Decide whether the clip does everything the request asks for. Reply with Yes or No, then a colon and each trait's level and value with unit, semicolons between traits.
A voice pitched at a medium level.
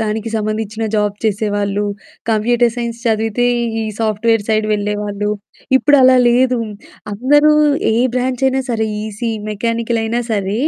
No: high, 225 Hz